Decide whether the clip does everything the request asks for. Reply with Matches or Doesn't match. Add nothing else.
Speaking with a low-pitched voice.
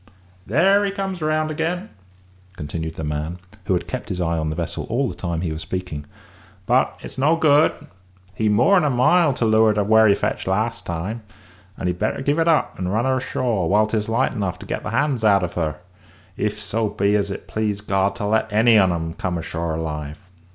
Matches